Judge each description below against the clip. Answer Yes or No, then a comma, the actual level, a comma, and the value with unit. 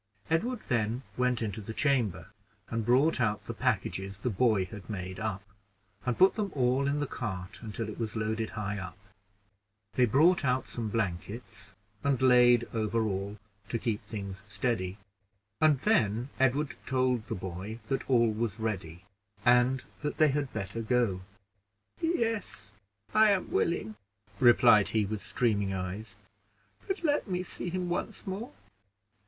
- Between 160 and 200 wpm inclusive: No, average, 150 wpm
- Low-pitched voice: Yes, low, 115 Hz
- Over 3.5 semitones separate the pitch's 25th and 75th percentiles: Yes, average, 4.6 semitones